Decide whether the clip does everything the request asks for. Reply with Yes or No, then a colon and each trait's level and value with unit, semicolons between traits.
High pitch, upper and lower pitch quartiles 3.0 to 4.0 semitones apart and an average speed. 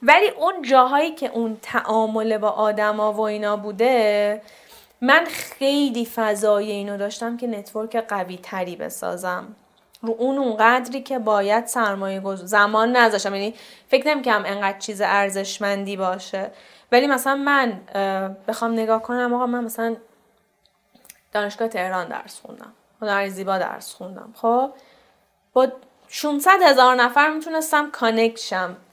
Yes: high, 225 Hz; average, 3.7 semitones; average, 130 wpm